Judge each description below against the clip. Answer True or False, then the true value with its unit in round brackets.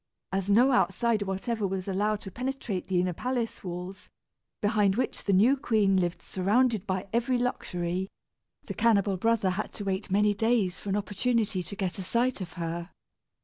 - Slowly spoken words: False (175 wpm)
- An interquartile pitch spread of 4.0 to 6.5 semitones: False (3.6 semitones)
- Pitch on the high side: True (200 Hz)